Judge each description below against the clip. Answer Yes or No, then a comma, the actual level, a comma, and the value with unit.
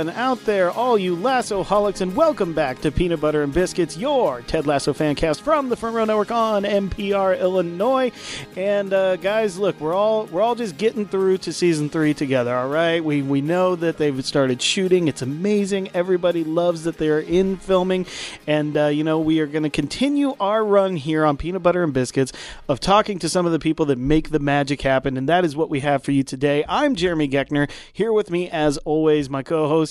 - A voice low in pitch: No, medium, 170 Hz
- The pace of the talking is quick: Yes, fast, 215 wpm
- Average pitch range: Yes, average, 4.7 semitones